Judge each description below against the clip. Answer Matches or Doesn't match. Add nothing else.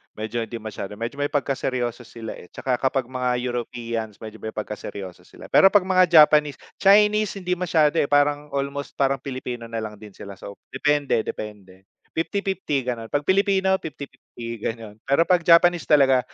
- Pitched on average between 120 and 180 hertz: Matches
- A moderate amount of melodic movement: Doesn't match